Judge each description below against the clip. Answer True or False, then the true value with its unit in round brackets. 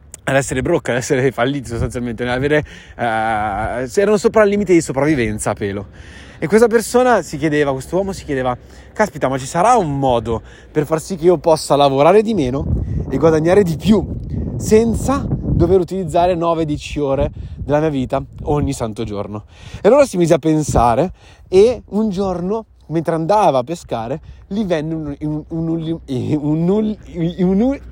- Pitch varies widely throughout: True (5.9 semitones)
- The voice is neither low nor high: True (155 Hz)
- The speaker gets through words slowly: False (170 wpm)